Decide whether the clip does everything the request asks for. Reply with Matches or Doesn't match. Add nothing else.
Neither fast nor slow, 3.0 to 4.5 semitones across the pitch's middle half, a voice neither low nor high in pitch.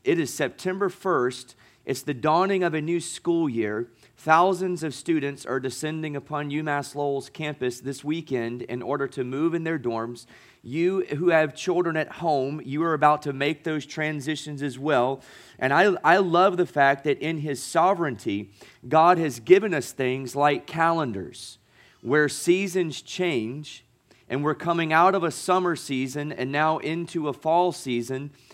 Matches